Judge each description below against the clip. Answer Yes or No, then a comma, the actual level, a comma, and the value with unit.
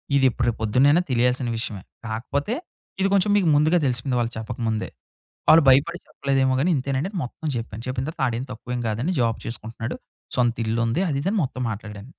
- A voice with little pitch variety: No, average, 3.6 semitones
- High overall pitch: No, low, 125 Hz